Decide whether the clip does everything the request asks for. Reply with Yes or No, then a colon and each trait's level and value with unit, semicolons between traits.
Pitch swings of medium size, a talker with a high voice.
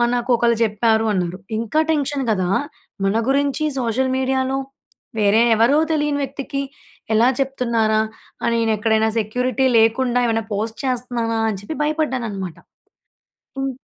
Yes: average, 3.3 semitones; high, 235 Hz